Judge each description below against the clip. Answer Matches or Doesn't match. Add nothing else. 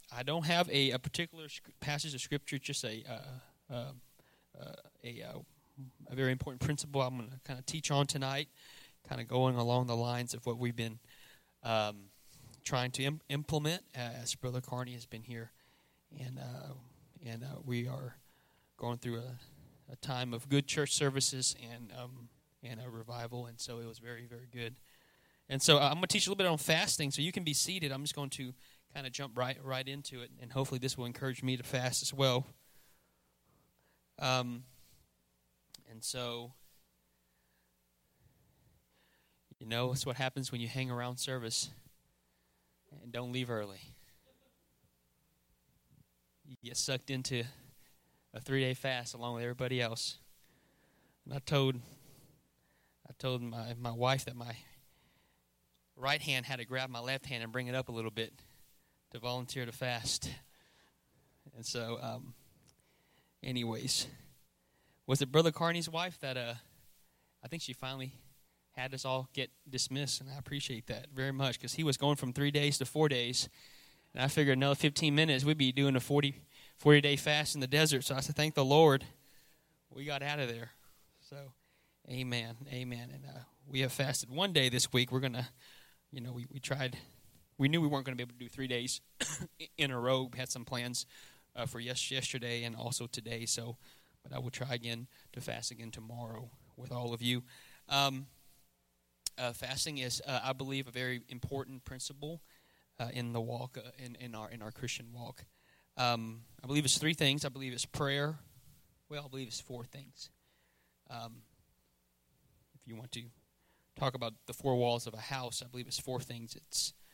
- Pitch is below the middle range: Matches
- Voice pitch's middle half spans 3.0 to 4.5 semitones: Doesn't match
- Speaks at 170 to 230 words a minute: Matches